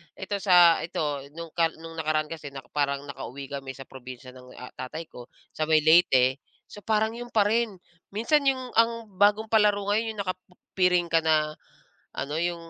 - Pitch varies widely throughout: Yes, wide, 6.6 semitones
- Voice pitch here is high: No, medium, 165 Hz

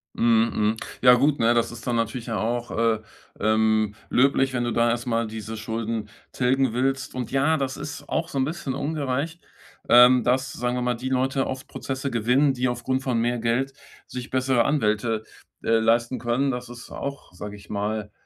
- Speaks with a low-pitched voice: Yes, low, 125 Hz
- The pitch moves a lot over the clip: No, narrow, 2.6 semitones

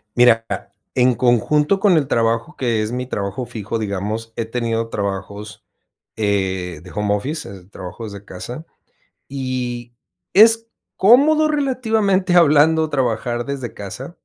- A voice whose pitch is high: No, low, 120 Hz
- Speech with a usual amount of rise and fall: No, wide, 6.5 semitones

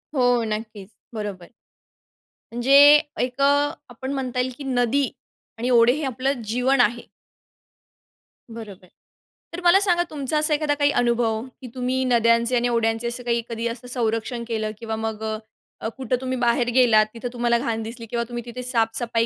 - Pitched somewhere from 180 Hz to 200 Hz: No, high, 240 Hz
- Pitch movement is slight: Yes, narrow, 2.2 semitones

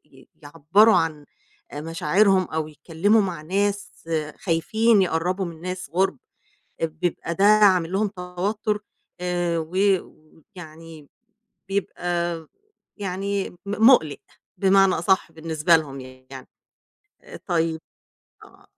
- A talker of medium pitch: Yes, medium, 175 Hz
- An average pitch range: Yes, average, 3.5 semitones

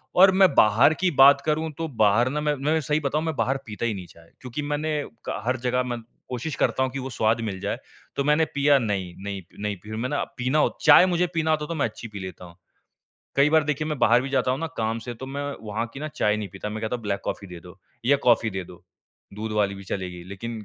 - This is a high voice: No, low, 125 Hz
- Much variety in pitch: Yes, wide, 5.9 semitones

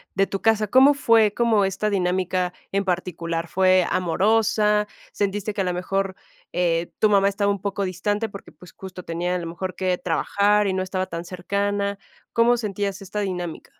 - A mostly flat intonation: Yes, narrow, 2.3 semitones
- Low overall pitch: No, high, 195 Hz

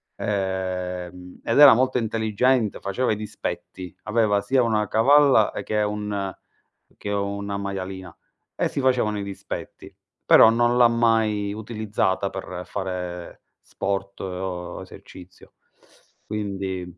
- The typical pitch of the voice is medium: No, low, 100 Hz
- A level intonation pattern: No, average, 3.0 semitones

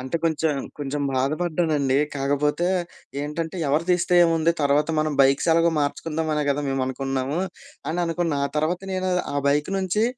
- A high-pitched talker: No, medium, 150 Hz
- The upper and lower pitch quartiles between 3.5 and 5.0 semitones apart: No, average, 3.0 semitones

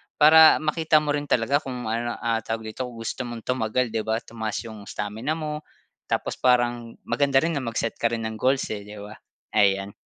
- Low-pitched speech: Yes, low, 120 Hz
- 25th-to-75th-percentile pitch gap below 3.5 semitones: No, average, 4.1 semitones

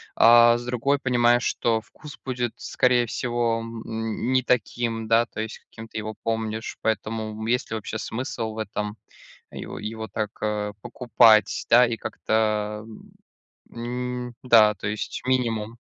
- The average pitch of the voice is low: Yes, low, 115 Hz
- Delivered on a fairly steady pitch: Yes, narrow, 1.8 semitones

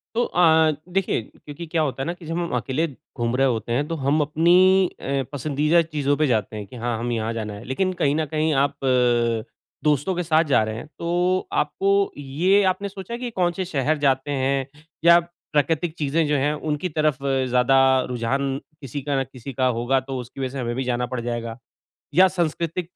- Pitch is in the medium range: Yes, medium, 145 Hz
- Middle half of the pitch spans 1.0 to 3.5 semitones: No, average, 4.6 semitones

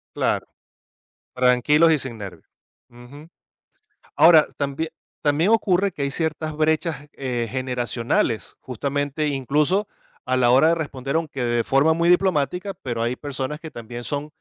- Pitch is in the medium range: Yes, medium, 145 Hz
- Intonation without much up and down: No, average, 4.1 semitones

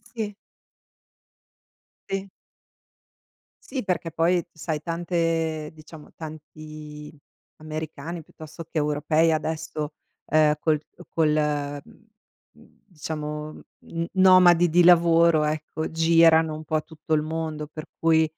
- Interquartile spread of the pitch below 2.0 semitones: Yes, narrow, 1.4 semitones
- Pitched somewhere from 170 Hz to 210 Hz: No, medium, 160 Hz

